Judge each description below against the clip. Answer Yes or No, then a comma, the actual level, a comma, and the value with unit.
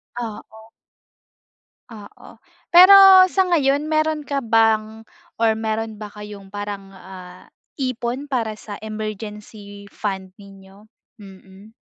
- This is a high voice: Yes, high, 215 Hz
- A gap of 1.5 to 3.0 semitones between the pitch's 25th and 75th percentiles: Yes, average, 2.7 semitones